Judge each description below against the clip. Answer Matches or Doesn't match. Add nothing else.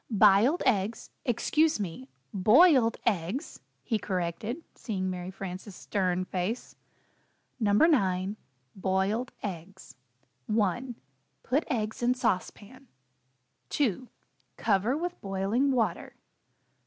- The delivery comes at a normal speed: Doesn't match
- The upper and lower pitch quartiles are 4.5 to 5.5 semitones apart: Matches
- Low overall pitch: Doesn't match